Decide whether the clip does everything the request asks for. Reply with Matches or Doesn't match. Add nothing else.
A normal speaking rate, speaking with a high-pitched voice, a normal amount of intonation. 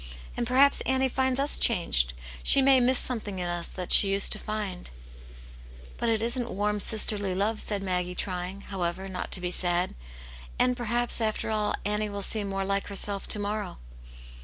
Matches